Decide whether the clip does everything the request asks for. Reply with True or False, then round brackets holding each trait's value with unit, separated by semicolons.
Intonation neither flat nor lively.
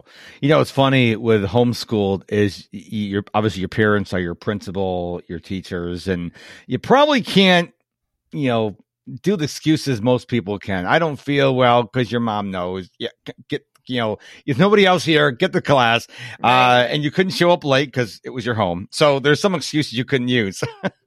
False (6.3 semitones)